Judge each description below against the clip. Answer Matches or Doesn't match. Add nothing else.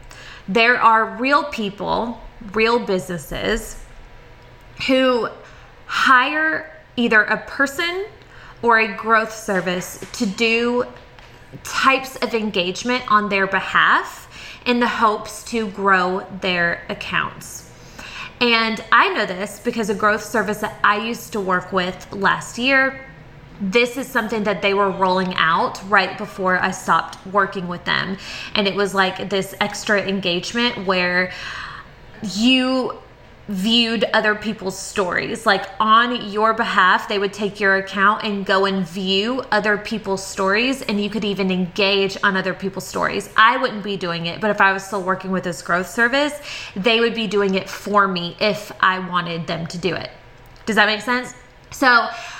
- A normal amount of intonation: Matches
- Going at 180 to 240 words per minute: Doesn't match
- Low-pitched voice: Doesn't match